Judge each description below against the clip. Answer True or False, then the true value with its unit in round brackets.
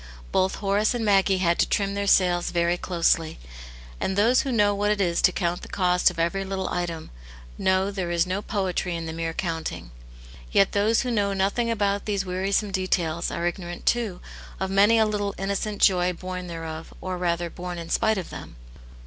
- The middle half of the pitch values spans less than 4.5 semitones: True (2.6 semitones)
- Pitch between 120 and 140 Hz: False (190 Hz)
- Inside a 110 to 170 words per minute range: False (195 wpm)